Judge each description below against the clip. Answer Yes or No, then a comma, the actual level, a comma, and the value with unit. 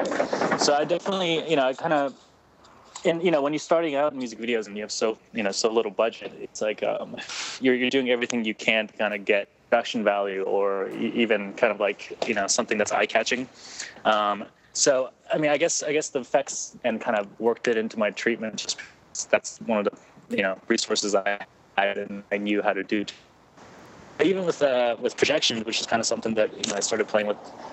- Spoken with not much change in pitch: No, average, 3.6 semitones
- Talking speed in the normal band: No, fast, 225 wpm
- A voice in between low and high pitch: No, low, 115 Hz